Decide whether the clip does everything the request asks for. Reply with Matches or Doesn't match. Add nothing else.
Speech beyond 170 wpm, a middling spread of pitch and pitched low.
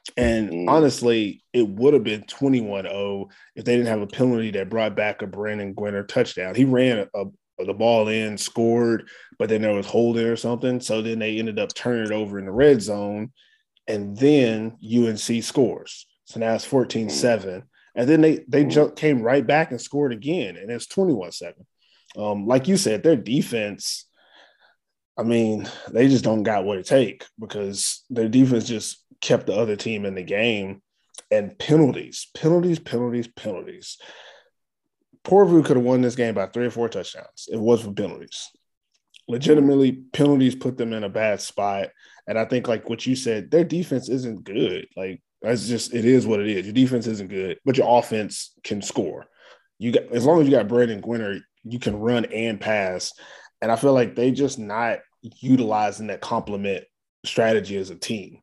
Matches